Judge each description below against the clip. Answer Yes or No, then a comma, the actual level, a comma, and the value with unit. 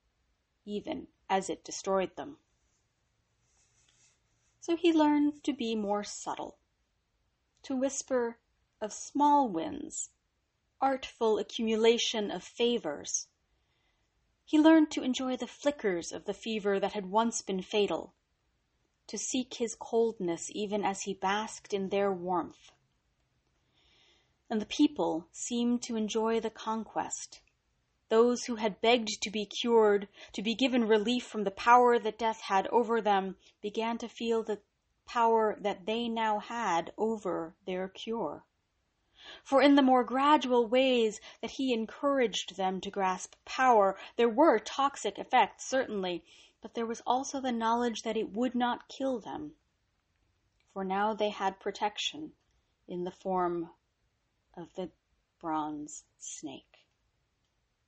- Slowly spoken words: Yes, slow, 130 wpm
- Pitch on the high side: Yes, high, 220 Hz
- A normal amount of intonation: Yes, average, 3.9 semitones